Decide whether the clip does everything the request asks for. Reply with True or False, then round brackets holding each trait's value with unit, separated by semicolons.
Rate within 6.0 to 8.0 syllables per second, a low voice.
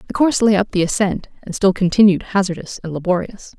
False (6.2 syllables/s; 190 Hz)